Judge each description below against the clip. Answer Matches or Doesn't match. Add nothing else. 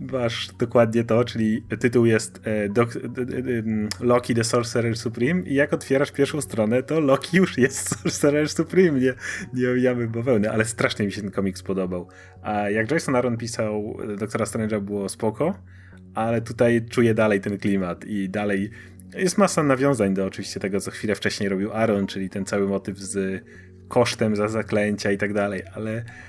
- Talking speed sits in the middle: Doesn't match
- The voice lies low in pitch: Matches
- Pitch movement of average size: Matches